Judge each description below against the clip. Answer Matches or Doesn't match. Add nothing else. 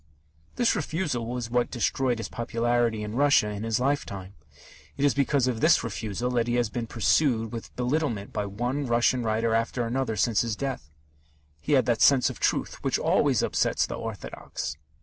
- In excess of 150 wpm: Matches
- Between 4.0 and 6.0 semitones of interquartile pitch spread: Doesn't match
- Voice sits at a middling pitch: Doesn't match